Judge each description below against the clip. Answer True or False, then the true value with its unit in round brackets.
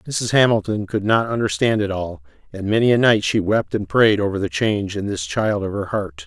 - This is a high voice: False (105 Hz)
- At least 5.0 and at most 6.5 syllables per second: True (5.2 syllables/s)